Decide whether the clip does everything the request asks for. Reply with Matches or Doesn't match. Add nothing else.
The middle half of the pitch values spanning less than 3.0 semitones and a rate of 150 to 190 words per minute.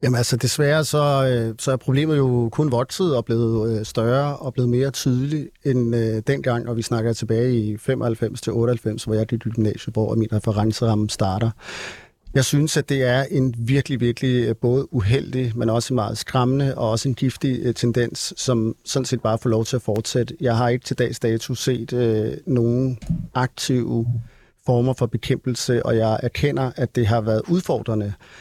Matches